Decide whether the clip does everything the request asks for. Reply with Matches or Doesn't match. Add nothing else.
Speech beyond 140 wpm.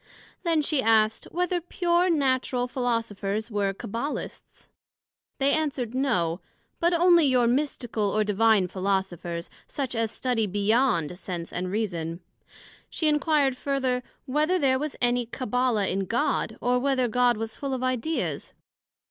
Doesn't match